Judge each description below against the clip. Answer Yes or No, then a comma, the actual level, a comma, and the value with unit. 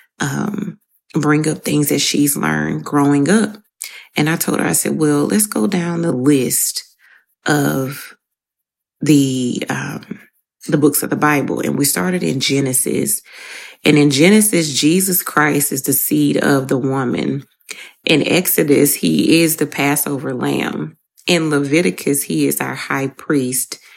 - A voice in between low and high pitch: Yes, medium, 145 Hz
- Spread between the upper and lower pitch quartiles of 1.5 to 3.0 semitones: No, average, 3.8 semitones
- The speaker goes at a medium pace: Yes, average, 150 wpm